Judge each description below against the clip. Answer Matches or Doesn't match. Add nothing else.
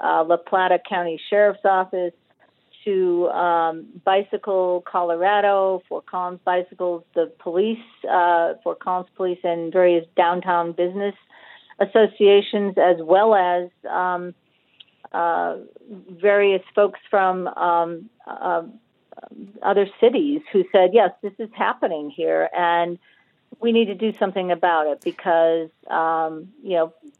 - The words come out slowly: Matches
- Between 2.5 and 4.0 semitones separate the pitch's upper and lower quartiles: Matches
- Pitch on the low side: Doesn't match